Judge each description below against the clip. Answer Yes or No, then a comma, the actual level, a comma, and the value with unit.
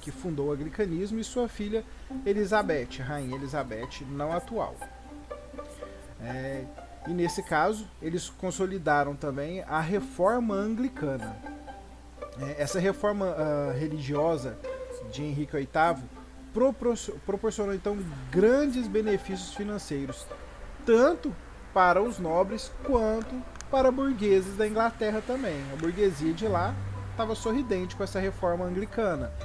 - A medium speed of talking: No, slow, 115 wpm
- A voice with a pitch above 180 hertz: Yes, high, 190 Hz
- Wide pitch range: Yes, wide, 7.2 semitones